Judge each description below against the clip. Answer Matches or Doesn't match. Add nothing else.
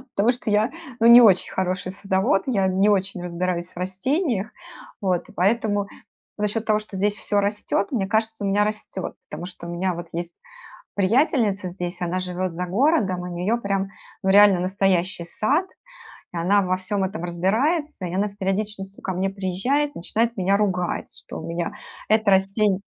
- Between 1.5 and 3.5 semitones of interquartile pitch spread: Matches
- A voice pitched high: Matches